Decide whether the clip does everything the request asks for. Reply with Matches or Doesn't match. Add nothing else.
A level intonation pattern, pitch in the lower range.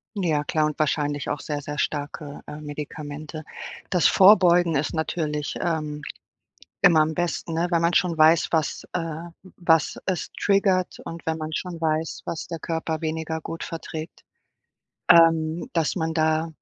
Doesn't match